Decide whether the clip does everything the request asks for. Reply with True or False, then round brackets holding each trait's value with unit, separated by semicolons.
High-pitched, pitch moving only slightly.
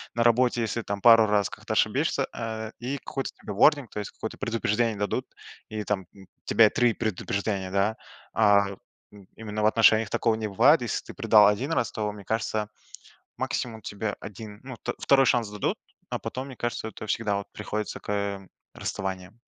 False (110 Hz; 2.2 semitones)